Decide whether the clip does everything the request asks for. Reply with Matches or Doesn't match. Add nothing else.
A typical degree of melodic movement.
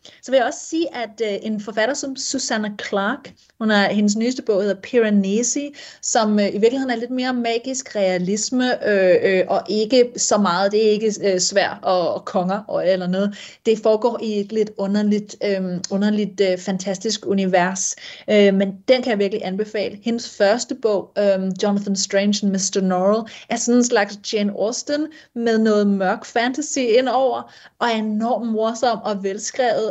Matches